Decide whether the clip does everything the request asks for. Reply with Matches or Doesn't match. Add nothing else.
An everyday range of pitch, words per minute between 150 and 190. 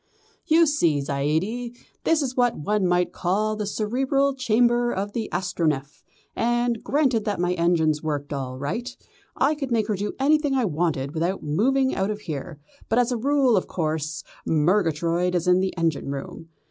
Doesn't match